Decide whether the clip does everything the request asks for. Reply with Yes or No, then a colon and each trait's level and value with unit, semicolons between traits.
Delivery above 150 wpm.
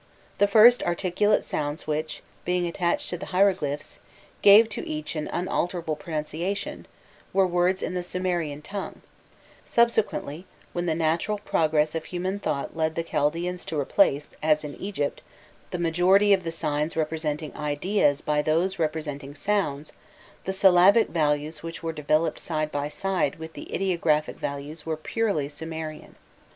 No: average, 145 wpm